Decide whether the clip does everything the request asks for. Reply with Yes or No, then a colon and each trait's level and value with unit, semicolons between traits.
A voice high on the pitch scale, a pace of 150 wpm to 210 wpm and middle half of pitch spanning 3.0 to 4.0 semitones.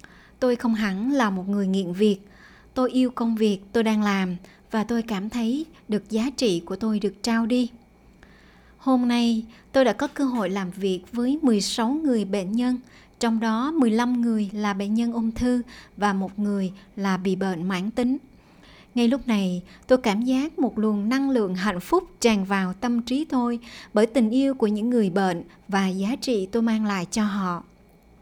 Yes: high, 225 Hz; average, 190 wpm; average, 3.5 semitones